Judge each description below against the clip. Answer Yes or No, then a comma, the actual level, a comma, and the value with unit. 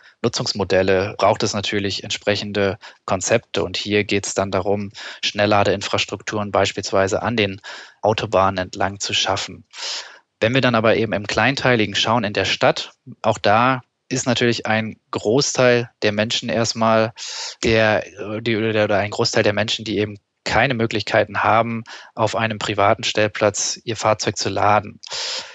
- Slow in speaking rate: No, average, 140 wpm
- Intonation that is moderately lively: No, narrow, 2.1 semitones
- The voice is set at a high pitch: No, low, 105 Hz